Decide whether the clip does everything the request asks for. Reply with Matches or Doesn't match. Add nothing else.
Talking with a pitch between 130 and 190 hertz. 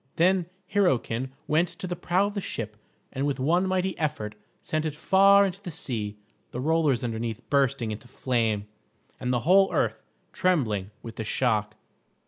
Matches